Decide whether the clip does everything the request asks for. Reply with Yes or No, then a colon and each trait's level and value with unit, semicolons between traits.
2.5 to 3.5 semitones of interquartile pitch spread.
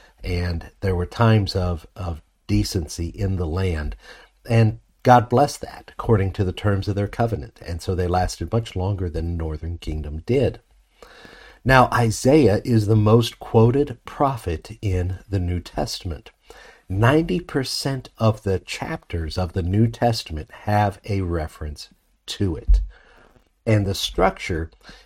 No: average, 4.5 semitones